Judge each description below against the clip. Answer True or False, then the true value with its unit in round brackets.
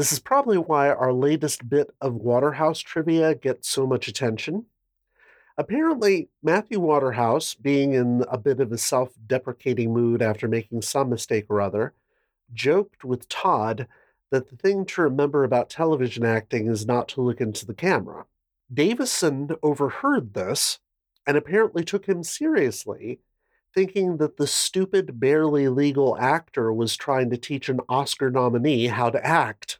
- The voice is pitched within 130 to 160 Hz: True (135 Hz)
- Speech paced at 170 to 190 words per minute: False (150 wpm)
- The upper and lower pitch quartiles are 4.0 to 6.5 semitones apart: True (4.5 semitones)